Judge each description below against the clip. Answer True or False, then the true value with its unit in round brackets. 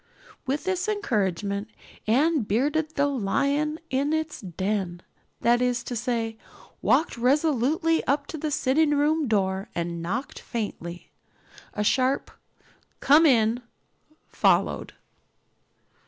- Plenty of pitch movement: True (6.1 semitones)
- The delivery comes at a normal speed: False (110 wpm)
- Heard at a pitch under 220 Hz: False (255 Hz)